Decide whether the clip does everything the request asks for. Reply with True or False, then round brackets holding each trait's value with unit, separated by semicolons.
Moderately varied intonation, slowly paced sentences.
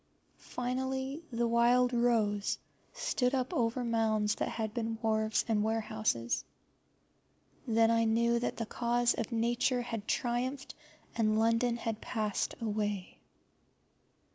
False (1.9 semitones; 120 wpm)